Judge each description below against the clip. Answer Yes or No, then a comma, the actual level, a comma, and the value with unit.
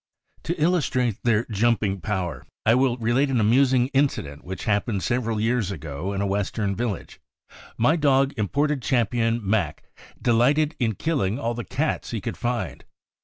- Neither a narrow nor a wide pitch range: Yes, average, 4.4 semitones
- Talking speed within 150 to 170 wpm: Yes, average, 155 wpm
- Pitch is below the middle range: Yes, low, 120 Hz